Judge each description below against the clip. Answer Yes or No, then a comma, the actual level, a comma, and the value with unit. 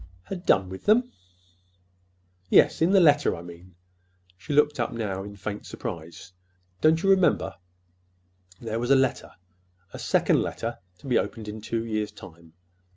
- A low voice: Yes, low, 105 Hz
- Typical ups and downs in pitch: No, wide, 7.6 semitones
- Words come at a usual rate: Yes, average, 155 wpm